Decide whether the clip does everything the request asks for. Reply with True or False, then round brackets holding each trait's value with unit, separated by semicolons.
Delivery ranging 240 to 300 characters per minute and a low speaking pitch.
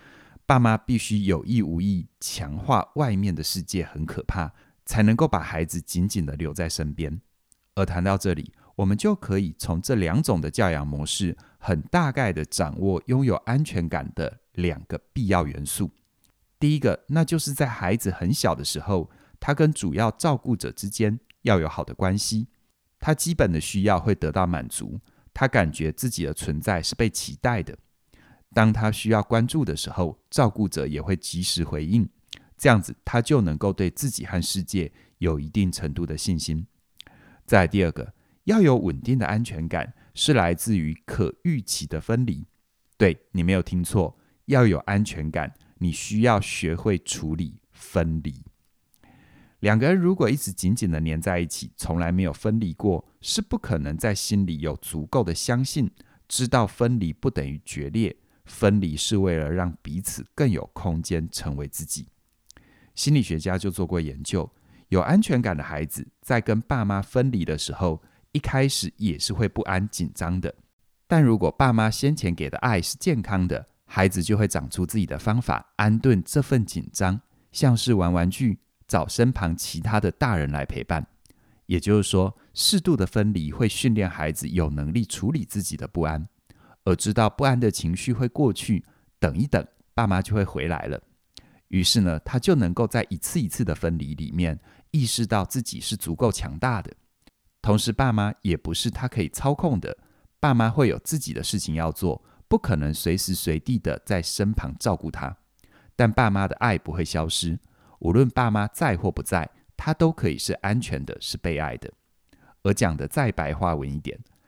True (260 characters per minute; 95 Hz)